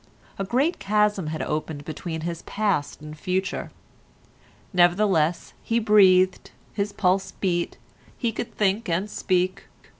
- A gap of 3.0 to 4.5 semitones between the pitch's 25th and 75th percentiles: Yes, average, 3.5 semitones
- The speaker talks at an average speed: No, slow, 125 wpm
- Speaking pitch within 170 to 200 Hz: Yes, medium, 185 Hz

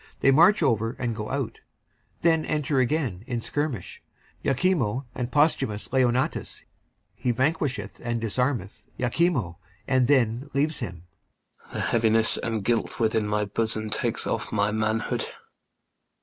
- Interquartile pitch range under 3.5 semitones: No, average, 4.1 semitones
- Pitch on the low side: Yes, low, 120 Hz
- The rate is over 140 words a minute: No, slow, 135 wpm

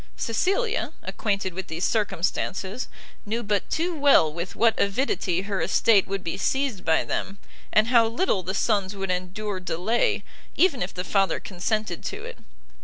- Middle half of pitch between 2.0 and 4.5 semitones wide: Yes, average, 3.9 semitones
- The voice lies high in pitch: Yes, high, 200 Hz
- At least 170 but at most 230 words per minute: No, average, 160 wpm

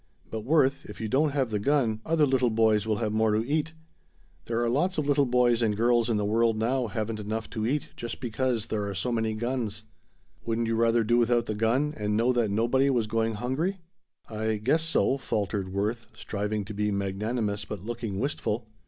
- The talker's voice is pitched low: Yes, low, 115 Hz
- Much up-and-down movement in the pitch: No, average, 2.9 semitones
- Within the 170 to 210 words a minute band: Yes, fast, 205 wpm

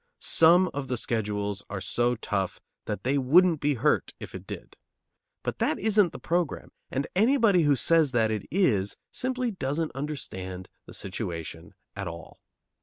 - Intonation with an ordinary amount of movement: No, wide, 8.7 semitones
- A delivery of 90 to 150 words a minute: No, average, 160 wpm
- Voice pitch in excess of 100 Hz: Yes, low, 135 Hz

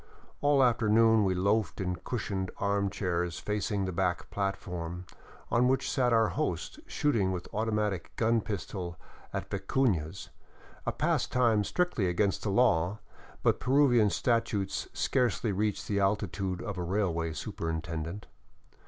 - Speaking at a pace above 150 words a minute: No, slow, 135 wpm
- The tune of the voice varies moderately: Yes, average, 3.9 semitones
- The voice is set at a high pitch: No, low, 100 Hz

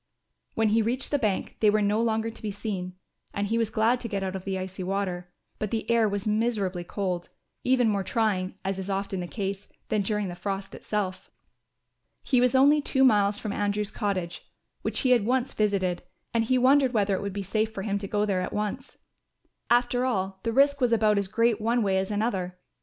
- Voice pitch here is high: Yes, high, 210 Hz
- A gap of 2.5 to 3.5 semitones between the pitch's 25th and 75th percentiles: Yes, average, 3.0 semitones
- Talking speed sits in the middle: No, fast, 215 wpm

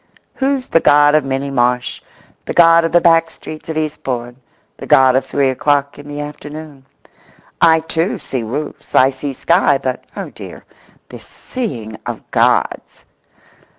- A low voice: No, medium, 145 Hz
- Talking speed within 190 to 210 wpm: No, average, 150 wpm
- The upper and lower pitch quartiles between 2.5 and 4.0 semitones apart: Yes, average, 3.5 semitones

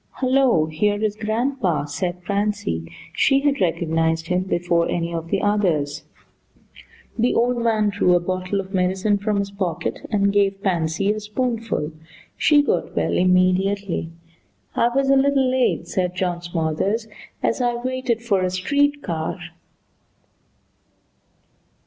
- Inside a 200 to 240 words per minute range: No, slow, 135 wpm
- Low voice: No, high, 200 Hz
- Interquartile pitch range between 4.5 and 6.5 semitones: Yes, average, 4.9 semitones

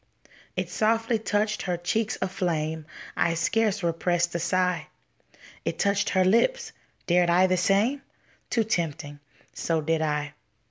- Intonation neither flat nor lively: Yes, average, 4.3 semitones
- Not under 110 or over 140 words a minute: Yes, slow, 135 wpm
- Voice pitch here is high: No, medium, 180 Hz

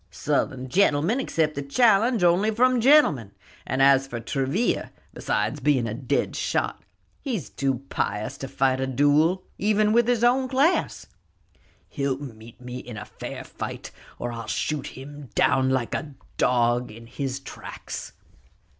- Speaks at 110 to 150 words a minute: Yes, average, 145 wpm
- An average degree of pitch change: No, wide, 8.7 semitones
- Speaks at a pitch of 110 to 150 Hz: Yes, medium, 140 Hz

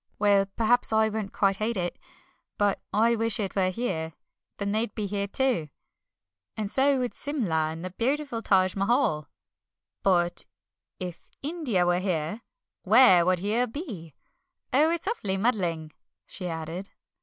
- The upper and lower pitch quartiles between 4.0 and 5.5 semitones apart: Yes, average, 4.7 semitones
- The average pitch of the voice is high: Yes, high, 200 Hz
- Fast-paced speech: No, average, 145 wpm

